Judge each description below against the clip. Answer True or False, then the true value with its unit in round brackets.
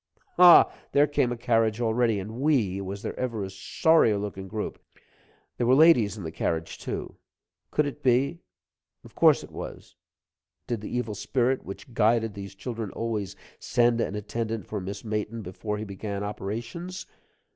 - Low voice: True (110 Hz)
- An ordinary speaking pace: True (165 wpm)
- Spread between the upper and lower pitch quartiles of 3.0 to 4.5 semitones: True (3.3 semitones)